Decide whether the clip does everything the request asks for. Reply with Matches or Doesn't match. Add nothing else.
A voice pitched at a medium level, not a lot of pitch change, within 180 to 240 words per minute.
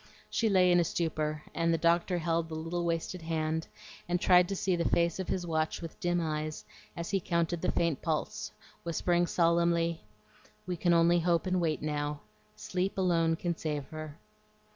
Matches